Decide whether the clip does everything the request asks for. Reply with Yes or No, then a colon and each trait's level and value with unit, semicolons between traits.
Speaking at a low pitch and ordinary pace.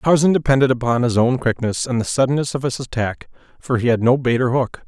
No: low, 125 Hz; fast, 235 wpm